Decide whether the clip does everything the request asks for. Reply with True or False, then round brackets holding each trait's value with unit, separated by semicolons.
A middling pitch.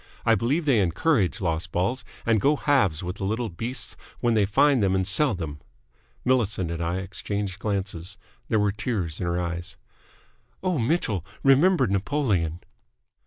False (100 Hz)